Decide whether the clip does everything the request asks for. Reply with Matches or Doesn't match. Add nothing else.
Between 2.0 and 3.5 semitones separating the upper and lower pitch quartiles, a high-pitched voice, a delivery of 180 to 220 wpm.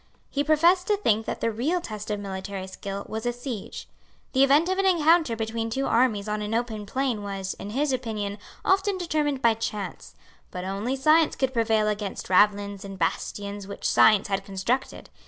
Doesn't match